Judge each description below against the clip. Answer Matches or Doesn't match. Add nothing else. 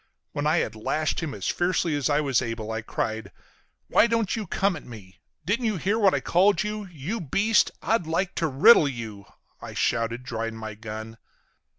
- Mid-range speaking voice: Matches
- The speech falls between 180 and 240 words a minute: Matches